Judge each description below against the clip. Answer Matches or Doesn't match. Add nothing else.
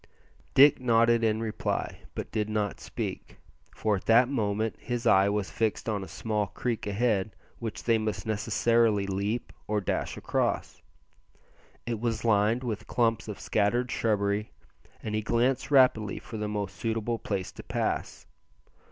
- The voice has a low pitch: Matches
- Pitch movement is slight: Matches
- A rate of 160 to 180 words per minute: Doesn't match